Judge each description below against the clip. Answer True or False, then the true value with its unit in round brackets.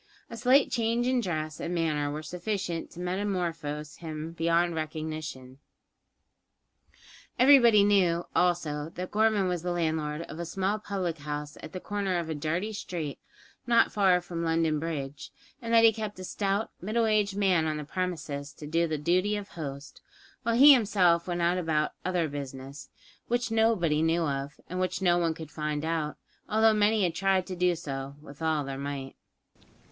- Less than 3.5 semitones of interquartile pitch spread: False (4.6 semitones)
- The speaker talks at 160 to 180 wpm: True (170 wpm)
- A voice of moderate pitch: True (170 Hz)